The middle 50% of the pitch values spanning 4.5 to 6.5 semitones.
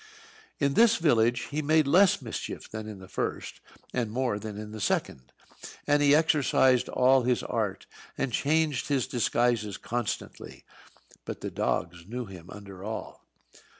Yes: average, 5.2 semitones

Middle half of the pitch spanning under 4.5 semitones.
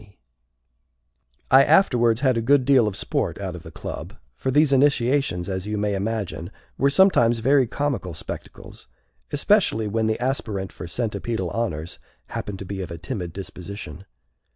No: wide, 5.5 semitones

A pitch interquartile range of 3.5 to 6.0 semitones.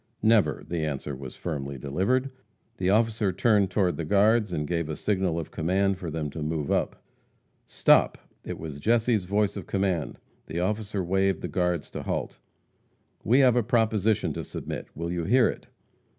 Yes: average, 4.7 semitones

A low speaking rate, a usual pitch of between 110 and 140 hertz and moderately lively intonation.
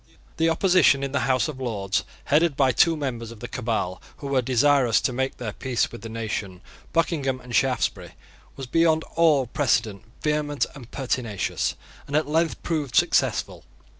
No: average, 165 wpm; low, 135 Hz; average, 4.4 semitones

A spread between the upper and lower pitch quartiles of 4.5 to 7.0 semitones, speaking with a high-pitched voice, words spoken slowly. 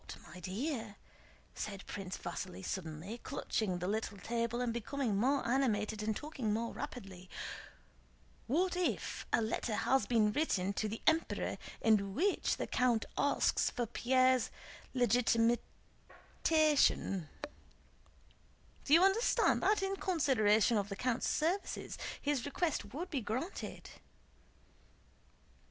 Yes: wide, 5.4 semitones; high, 235 Hz; slow, 120 wpm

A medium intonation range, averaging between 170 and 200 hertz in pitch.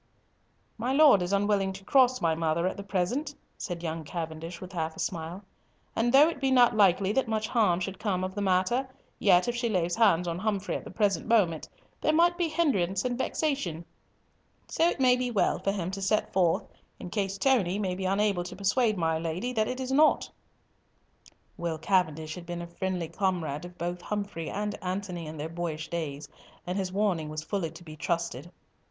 Yes: average, 4.3 semitones; high, 190 Hz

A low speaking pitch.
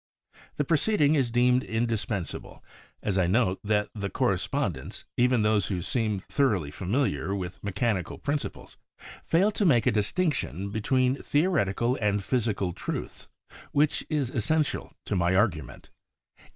Yes: low, 110 Hz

